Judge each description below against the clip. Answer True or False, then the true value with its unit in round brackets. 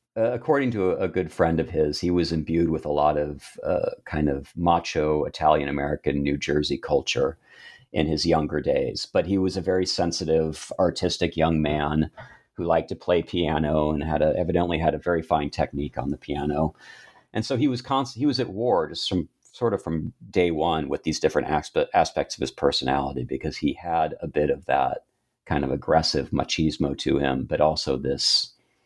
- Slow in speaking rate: False (195 wpm)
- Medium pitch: False (80 Hz)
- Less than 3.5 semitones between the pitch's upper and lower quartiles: True (2.9 semitones)